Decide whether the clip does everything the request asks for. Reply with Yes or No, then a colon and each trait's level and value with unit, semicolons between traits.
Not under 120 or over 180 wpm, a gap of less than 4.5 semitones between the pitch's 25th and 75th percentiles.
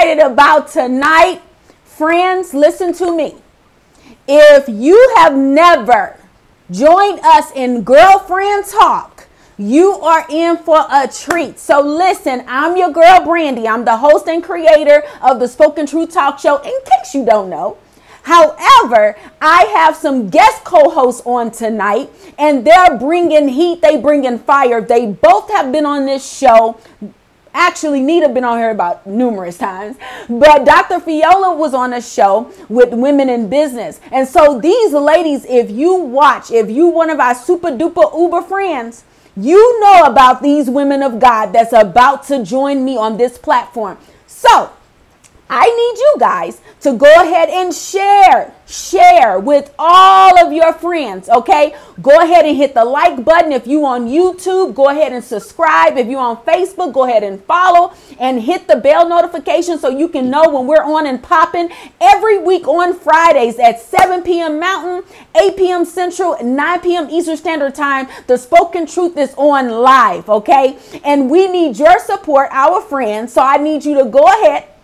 No: average, 165 wpm; average, 4.8 semitones